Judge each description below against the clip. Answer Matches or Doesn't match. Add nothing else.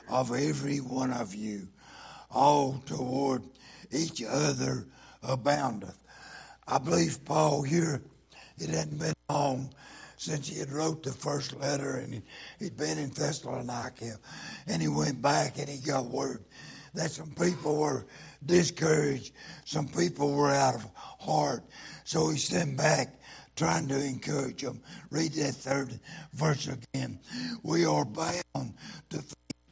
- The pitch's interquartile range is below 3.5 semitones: Matches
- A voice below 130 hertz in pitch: Doesn't match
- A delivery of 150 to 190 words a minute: Doesn't match